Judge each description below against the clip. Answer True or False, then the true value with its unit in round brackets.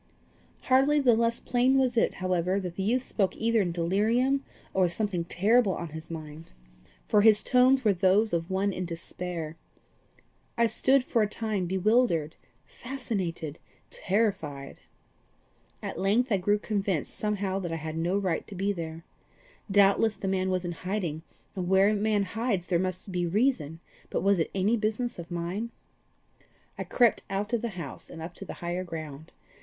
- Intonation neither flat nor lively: True (4.4 semitones)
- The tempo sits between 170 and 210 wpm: True (175 wpm)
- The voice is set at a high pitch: True (195 Hz)